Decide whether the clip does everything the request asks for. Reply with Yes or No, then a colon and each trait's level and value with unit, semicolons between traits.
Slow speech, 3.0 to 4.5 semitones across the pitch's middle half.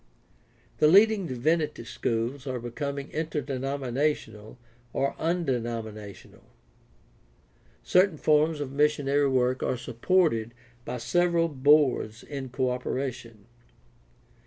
Yes: slow, 95 wpm; average, 3.9 semitones